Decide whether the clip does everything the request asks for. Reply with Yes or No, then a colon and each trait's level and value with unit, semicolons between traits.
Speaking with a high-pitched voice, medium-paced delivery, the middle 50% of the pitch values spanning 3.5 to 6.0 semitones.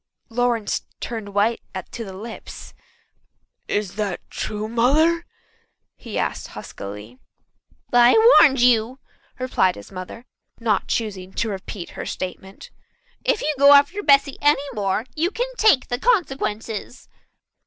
No: high, 230 Hz; slow, 125 wpm; wide, 5.6 semitones